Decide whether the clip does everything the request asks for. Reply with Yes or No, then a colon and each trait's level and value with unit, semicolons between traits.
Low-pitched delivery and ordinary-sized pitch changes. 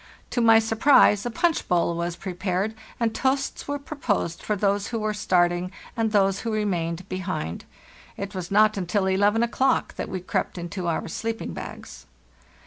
No: high, 200 Hz; average, 3.8 semitones